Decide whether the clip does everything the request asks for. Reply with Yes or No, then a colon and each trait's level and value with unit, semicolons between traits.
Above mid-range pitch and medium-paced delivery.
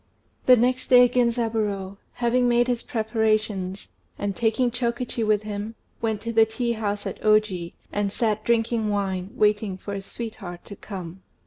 Yes: high, 220 Hz; average, 155 wpm